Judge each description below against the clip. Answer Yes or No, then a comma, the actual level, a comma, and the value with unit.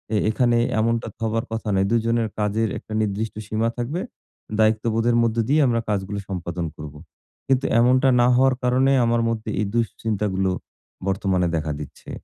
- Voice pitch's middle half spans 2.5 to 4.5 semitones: Yes, average, 2.9 semitones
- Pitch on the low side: Yes, low, 110 Hz